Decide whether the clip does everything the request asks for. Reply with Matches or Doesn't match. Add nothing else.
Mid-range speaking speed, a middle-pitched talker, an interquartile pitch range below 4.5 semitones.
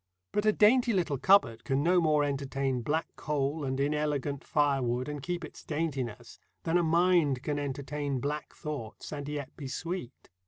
Matches